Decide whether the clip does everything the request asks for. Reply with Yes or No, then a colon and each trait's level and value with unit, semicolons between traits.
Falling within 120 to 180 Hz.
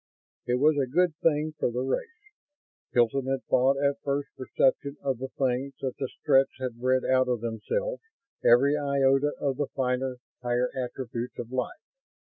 Yes: low, 135 Hz